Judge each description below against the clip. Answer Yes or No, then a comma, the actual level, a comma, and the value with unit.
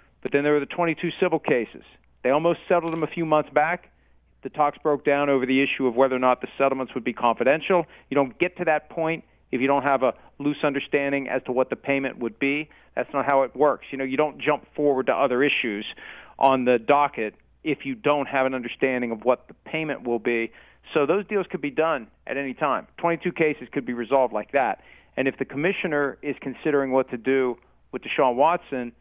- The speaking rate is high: Yes, fast, 225 wpm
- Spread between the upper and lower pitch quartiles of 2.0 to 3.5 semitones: Yes, average, 2.7 semitones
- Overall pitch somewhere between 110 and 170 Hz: Yes, medium, 140 Hz